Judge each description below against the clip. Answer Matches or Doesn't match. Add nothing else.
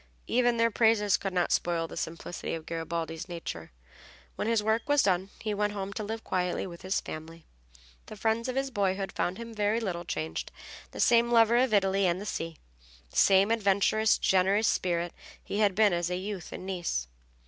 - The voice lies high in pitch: Matches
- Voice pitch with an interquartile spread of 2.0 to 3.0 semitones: Doesn't match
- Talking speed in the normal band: Matches